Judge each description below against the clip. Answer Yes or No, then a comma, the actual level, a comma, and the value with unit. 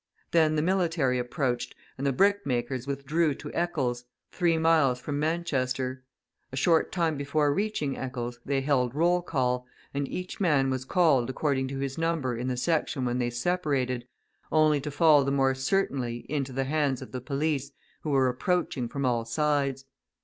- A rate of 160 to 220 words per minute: Yes, average, 170 wpm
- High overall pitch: No, medium, 140 Hz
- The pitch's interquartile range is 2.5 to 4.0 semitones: Yes, average, 3.6 semitones